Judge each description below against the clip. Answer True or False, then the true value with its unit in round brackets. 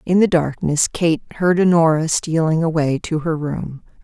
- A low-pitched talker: False (160 Hz)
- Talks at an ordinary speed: True (165 wpm)